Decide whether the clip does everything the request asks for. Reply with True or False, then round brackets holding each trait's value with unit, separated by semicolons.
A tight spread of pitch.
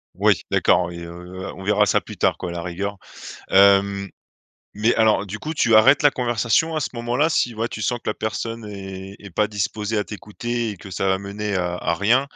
False (3.1 semitones)